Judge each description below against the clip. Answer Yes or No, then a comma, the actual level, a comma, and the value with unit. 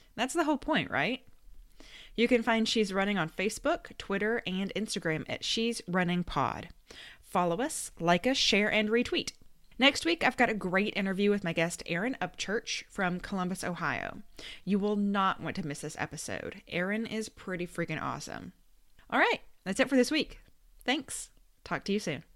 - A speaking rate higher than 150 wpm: Yes, average, 175 wpm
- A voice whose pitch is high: Yes, high, 205 Hz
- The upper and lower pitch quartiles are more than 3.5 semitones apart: Yes, average, 4.6 semitones